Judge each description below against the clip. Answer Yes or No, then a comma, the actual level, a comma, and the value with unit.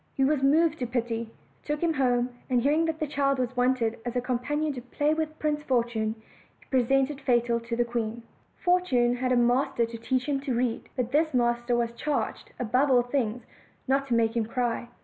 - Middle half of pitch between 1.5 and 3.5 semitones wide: Yes, average, 2.9 semitones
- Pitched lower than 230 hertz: No, very high, 250 Hz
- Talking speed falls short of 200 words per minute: No, fast, 205 wpm